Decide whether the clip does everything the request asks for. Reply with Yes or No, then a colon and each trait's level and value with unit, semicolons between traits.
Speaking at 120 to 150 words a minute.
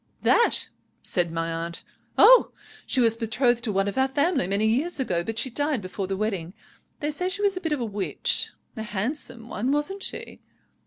No: average, 200 wpm